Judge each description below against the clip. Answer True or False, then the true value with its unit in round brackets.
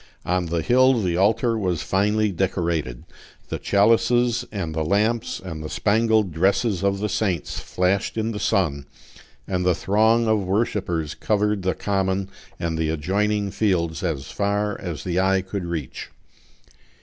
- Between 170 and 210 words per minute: False (150 wpm)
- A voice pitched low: True (95 Hz)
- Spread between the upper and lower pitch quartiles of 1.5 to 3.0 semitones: False (3.7 semitones)